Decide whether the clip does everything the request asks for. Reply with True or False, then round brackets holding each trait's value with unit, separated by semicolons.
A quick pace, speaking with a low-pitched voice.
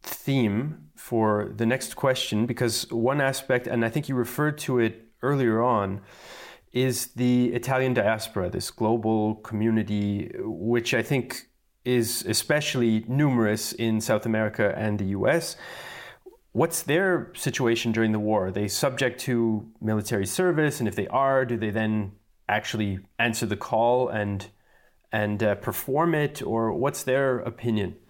False (145 wpm; 115 Hz)